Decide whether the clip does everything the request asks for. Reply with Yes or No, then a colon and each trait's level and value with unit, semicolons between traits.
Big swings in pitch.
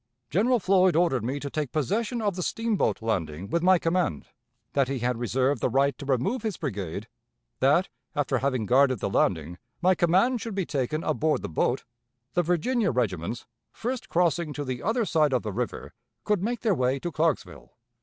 Yes: wide, 6.9 semitones